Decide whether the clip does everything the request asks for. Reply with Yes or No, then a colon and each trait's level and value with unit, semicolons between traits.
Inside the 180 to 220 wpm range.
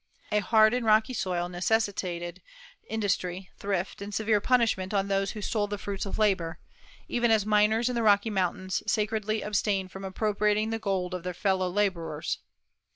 No: average, 165 wpm